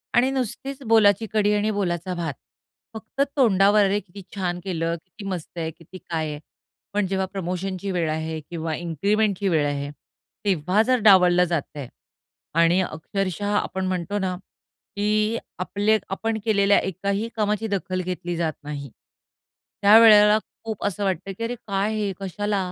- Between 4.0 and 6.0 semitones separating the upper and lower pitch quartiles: No, average, 3.2 semitones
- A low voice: No, high, 195 Hz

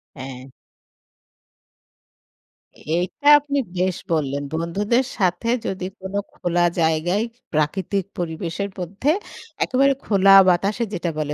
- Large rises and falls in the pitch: No, average, 3.6 semitones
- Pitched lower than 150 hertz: No, medium, 180 Hz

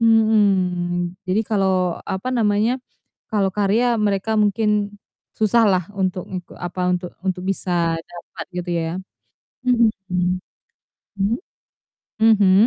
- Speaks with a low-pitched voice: No, high, 195 Hz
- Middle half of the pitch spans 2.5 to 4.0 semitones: Yes, average, 2.8 semitones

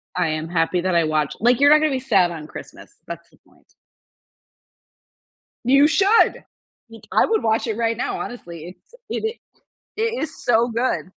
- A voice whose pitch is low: No, high, 230 Hz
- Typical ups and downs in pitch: No, wide, 8.6 semitones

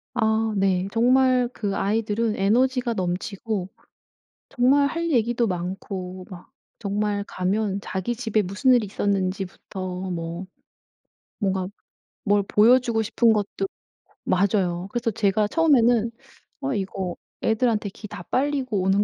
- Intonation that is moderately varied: Yes, average, 3.7 semitones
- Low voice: No, high, 210 Hz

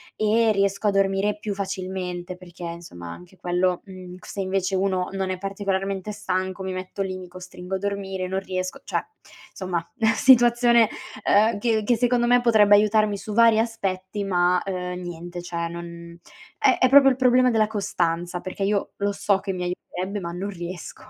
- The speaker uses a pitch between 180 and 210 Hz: Yes, high, 190 Hz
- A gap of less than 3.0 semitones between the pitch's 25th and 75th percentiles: Yes, narrow, 2.5 semitones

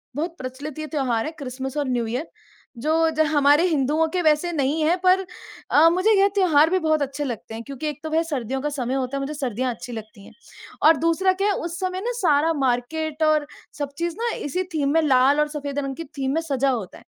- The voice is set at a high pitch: Yes, very high, 295 Hz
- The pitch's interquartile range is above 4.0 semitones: No, average, 3.7 semitones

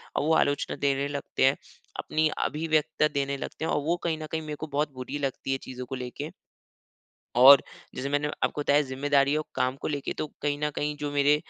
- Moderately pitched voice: Yes, medium, 145 Hz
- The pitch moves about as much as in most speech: No, narrow, 1.5 semitones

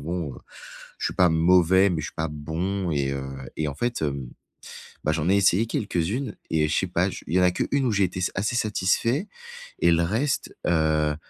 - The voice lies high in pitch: No, very low, 90 Hz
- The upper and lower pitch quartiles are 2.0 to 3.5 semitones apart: No, average, 4.3 semitones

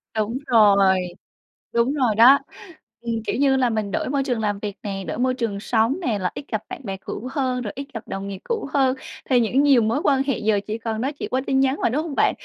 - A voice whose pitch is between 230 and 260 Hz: Yes, high, 240 Hz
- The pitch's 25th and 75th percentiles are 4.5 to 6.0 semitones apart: No, average, 4.1 semitones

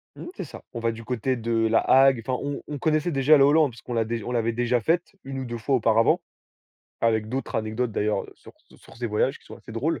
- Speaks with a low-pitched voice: Yes, low, 120 Hz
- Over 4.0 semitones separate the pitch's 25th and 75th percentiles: No, average, 3.1 semitones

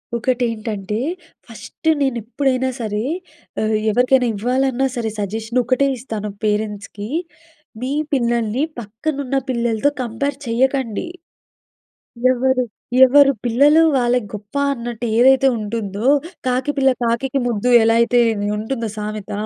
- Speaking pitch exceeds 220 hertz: Yes, high, 240 Hz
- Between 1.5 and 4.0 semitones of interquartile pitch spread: Yes, average, 3.2 semitones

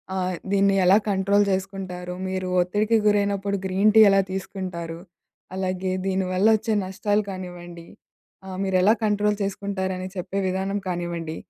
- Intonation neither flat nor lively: No, narrow, 1.6 semitones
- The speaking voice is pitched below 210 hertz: Yes, high, 190 Hz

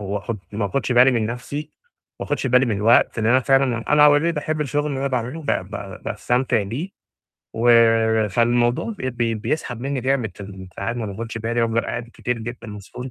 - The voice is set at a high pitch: No, low, 120 Hz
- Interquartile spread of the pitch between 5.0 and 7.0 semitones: No, average, 3.1 semitones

